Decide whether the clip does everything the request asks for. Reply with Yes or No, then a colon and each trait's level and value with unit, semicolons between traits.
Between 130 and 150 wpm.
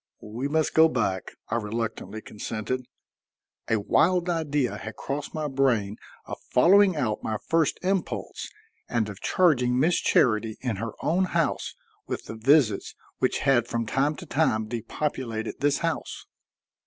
Yes: average, 145 wpm